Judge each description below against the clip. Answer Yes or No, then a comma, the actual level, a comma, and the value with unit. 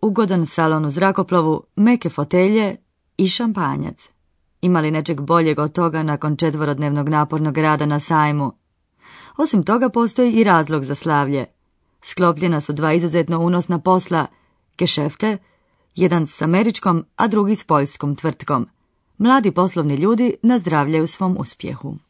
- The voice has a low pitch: No, medium, 170 Hz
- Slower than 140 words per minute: Yes, average, 130 wpm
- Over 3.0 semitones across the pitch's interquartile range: Yes, average, 4.1 semitones